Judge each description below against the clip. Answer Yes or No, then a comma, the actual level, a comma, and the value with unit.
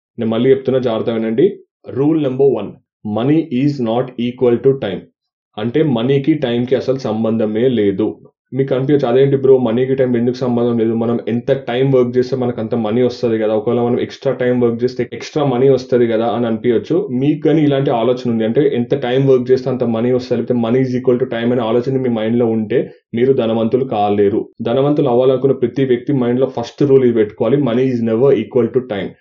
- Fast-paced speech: Yes, fast, 195 wpm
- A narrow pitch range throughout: Yes, narrow, 2.2 semitones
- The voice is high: No, low, 125 Hz